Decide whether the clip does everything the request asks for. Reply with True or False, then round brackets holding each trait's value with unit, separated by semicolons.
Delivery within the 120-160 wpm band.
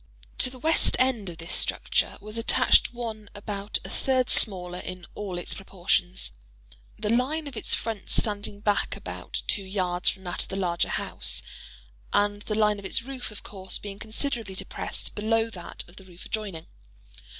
False (170 wpm)